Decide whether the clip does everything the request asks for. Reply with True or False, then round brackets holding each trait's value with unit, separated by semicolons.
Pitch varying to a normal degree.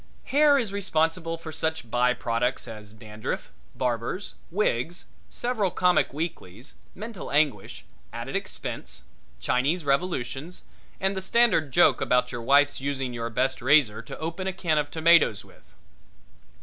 False (6.5 semitones)